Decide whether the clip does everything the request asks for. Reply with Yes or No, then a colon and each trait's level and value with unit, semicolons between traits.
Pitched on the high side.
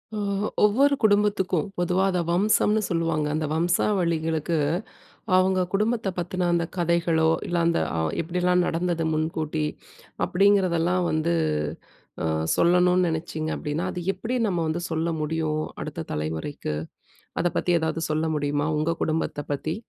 No: medium, 170 Hz